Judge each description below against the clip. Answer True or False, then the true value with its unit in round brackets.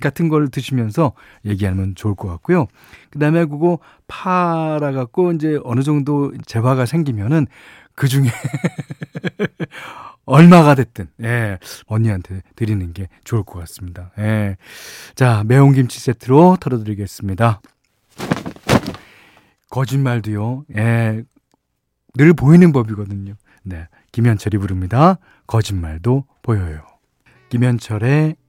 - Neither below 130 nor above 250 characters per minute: True (245 characters per minute)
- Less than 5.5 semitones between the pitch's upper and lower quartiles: False (5.9 semitones)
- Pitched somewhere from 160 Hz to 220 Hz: False (125 Hz)